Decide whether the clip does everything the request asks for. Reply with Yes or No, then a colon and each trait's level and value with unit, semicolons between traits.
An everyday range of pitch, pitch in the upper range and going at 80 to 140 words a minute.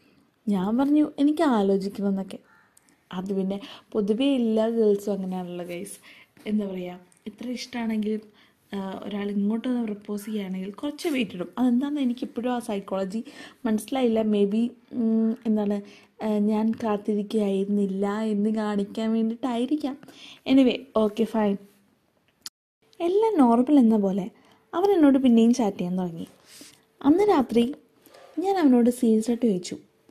Yes: average, 3.5 semitones; high, 220 Hz; average, 110 wpm